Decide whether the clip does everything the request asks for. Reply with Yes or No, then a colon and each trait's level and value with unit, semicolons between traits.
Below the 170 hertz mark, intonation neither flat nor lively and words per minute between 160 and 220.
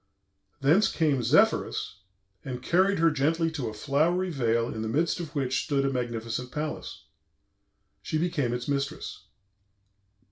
No: medium, 140 Hz; average, 4.9 semitones; average, 140 wpm